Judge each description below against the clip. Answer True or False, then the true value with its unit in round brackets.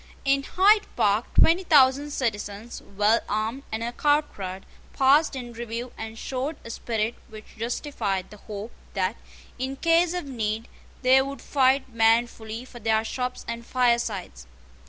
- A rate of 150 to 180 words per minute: False (140 wpm)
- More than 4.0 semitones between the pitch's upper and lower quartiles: False (3.7 semitones)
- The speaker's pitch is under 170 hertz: False (235 Hz)